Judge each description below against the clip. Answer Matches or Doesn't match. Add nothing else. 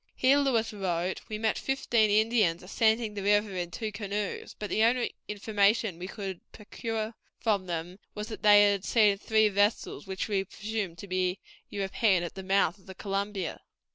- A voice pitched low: Doesn't match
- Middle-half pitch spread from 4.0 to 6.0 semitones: Doesn't match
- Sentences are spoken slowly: Doesn't match